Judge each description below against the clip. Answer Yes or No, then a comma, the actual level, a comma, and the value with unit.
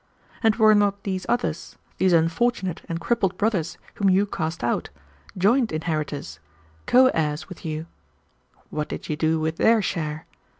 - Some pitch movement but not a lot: Yes, average, 4.7 semitones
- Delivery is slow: No, average, 155 wpm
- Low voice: No, medium, 180 Hz